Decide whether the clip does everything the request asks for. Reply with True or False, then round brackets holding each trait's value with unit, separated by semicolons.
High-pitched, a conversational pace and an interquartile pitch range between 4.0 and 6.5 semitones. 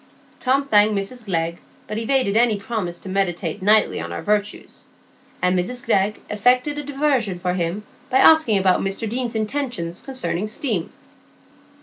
True (210 Hz; 150 wpm; 4.7 semitones)